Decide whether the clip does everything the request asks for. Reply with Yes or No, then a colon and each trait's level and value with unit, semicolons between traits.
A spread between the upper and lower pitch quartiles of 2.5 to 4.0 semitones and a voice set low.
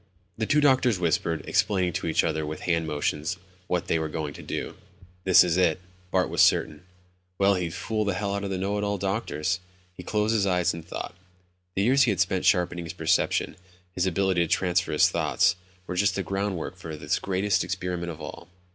Yes: average, 3.0 semitones; very low, 90 Hz